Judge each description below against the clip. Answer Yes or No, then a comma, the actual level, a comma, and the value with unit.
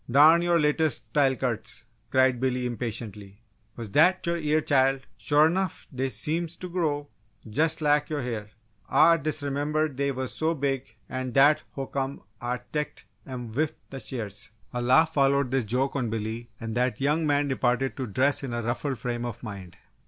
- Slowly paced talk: No, average, 175 wpm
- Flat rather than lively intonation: No, average, 3.7 semitones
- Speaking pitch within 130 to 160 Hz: Yes, low, 135 Hz